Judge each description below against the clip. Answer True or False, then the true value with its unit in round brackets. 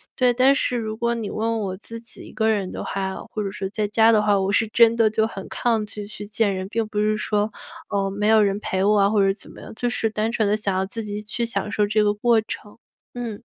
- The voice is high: True (215 Hz)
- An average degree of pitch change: False (1.7 semitones)